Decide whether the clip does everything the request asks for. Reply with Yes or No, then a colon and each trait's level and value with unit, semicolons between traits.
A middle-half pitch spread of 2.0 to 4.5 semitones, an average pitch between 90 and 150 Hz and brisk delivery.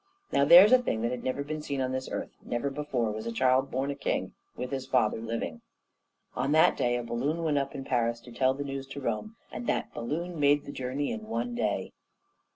Yes: average, 3.2 semitones; low, 135 Hz; fast, 230 wpm